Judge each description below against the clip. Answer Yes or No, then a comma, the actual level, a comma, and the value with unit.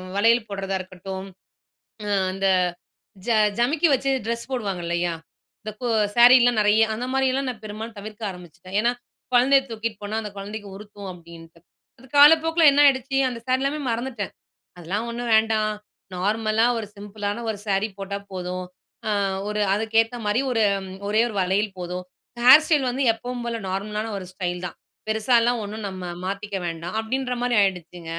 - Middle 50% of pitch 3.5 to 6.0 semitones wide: Yes, average, 3.8 semitones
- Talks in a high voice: Yes, high, 215 Hz